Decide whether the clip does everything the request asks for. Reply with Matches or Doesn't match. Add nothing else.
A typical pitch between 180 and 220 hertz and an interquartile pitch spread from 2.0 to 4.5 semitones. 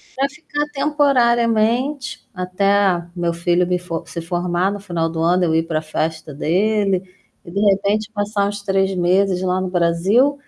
Matches